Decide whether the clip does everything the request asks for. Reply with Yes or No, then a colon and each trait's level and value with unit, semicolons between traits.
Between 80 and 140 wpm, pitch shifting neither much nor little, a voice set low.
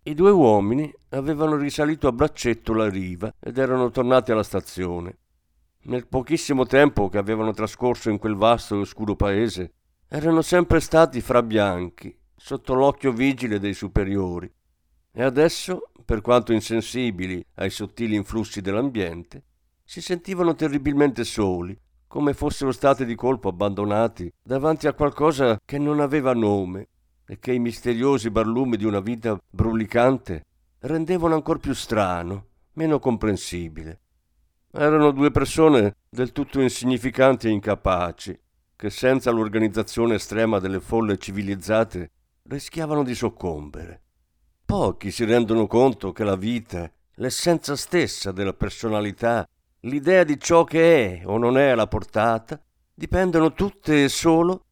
No: average, 130 wpm; wide, 6.1 semitones; low, 115 Hz